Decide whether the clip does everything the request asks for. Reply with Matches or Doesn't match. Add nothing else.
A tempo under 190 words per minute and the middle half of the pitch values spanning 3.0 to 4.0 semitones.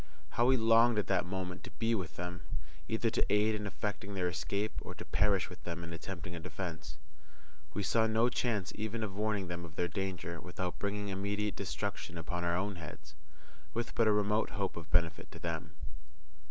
Doesn't match